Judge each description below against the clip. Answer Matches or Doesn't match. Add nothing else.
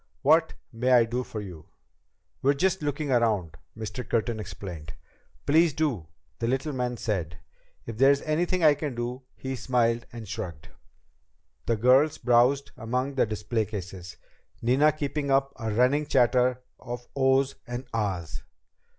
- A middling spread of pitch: Matches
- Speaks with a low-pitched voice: Matches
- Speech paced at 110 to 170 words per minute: Matches